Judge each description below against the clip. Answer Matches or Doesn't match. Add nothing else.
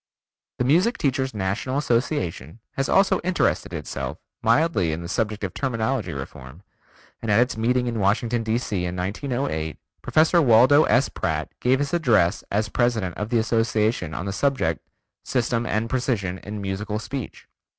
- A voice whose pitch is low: Matches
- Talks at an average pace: Matches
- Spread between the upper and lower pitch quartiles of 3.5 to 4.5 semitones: Doesn't match